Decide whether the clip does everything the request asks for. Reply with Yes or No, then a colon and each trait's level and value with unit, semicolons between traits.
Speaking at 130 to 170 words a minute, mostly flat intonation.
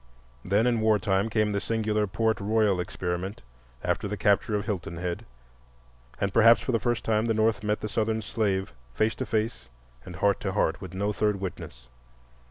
No: average, 185 wpm; narrow, 2.3 semitones